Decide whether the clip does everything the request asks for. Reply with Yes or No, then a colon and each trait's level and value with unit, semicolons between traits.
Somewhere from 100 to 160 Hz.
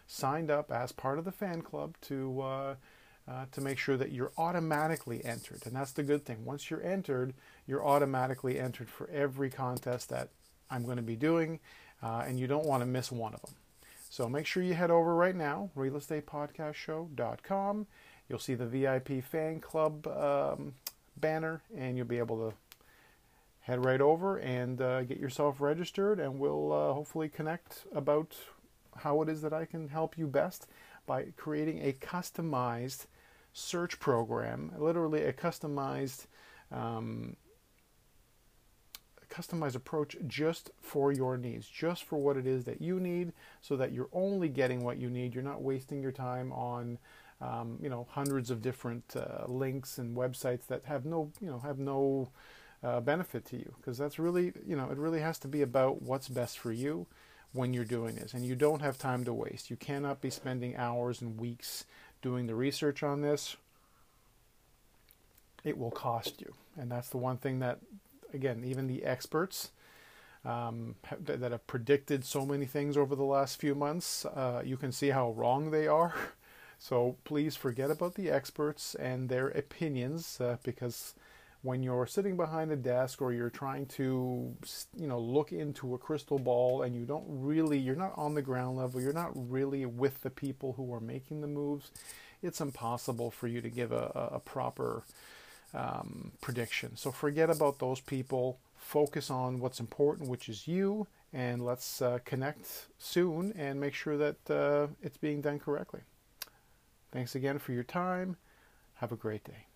Yes: low, 135 Hz